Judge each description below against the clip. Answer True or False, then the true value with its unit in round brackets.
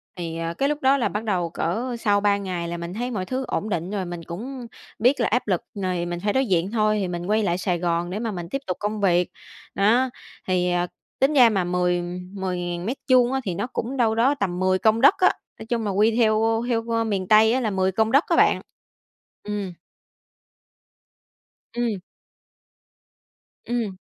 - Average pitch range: True (4.5 semitones)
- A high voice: True (205 Hz)